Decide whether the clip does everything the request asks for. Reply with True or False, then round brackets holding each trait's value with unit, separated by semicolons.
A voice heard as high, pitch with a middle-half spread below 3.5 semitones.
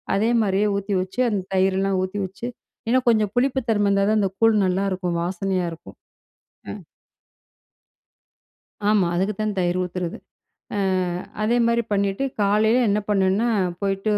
True (200 Hz; 2.4 semitones)